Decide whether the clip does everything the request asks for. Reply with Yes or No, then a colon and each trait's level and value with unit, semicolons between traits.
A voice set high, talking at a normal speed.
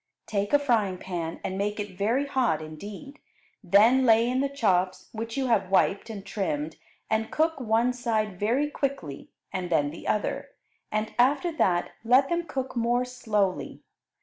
Yes: high, 220 Hz; average, 165 wpm